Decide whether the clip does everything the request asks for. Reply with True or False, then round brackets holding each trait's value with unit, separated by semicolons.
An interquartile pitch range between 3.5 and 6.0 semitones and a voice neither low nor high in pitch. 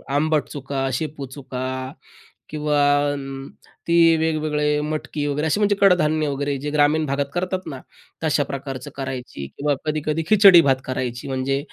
False (2.4 semitones; 150 Hz)